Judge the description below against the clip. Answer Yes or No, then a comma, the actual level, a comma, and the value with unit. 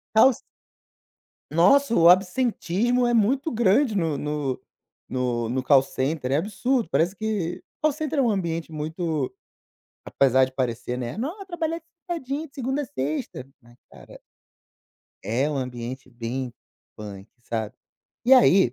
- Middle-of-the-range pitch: Yes, medium, 170 Hz